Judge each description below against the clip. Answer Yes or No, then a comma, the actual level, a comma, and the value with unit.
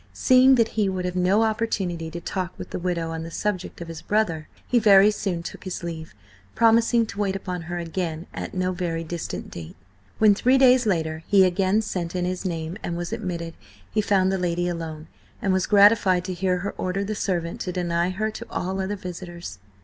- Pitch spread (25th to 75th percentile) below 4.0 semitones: Yes, average, 3.1 semitones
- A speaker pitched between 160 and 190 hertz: Yes, medium, 185 Hz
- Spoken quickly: Yes, fast, 210 wpm